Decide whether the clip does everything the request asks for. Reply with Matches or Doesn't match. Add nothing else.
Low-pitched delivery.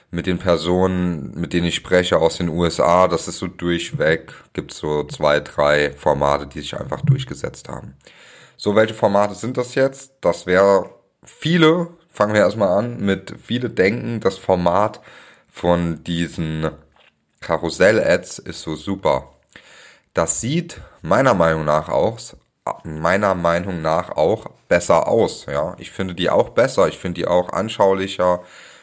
Matches